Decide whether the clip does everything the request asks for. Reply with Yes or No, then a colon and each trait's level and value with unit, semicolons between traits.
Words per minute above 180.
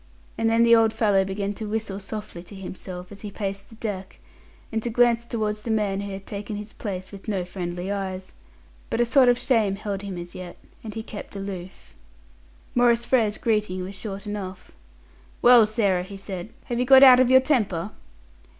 Yes: average, 195 wpm